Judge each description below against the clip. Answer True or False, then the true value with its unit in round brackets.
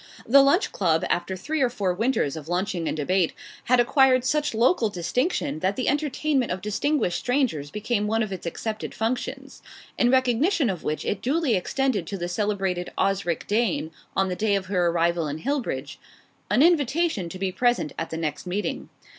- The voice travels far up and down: True (6.5 semitones)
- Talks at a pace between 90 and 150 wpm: False (180 wpm)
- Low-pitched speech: False (210 Hz)